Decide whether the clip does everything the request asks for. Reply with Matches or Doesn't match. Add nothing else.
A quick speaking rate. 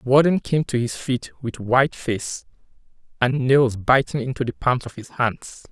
Doesn't match